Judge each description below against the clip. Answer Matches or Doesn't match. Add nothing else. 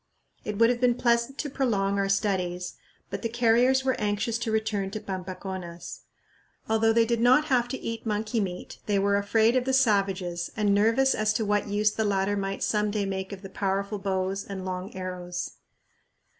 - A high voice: Matches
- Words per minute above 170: Matches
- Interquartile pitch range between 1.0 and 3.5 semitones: Matches